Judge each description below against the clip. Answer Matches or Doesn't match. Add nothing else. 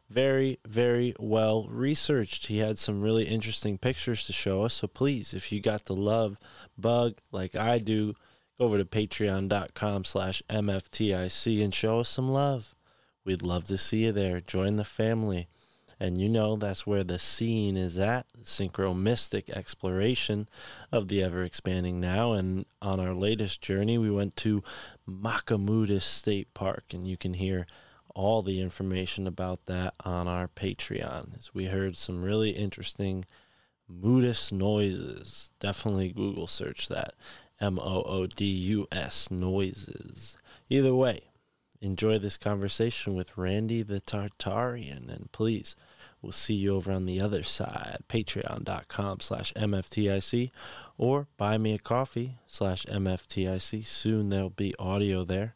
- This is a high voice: Doesn't match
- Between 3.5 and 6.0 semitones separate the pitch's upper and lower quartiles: Doesn't match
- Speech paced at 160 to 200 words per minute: Doesn't match